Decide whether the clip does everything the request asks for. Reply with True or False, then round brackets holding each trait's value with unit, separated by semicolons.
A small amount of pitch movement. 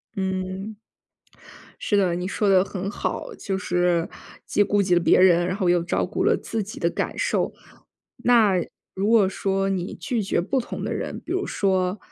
True (2.1 semitones)